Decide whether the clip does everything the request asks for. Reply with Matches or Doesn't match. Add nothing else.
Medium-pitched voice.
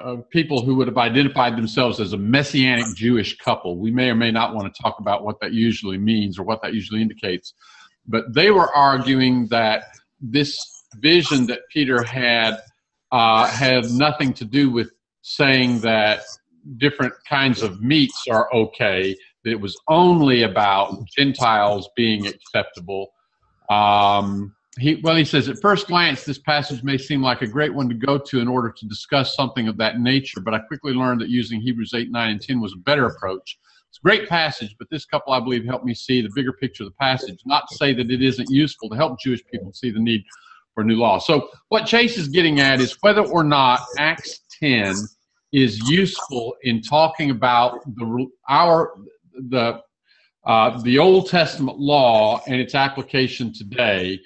Doesn't match